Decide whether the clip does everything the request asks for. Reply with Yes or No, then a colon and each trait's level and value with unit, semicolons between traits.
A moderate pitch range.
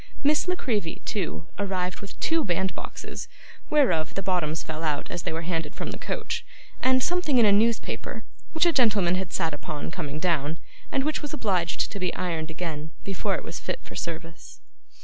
No: wide, 6.3 semitones